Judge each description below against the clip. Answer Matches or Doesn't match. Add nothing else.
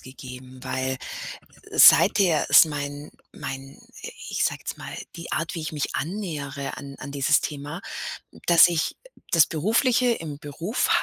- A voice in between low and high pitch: Matches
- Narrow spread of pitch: Doesn't match